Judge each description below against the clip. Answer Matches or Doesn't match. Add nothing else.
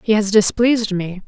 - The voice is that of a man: Doesn't match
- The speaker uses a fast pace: Doesn't match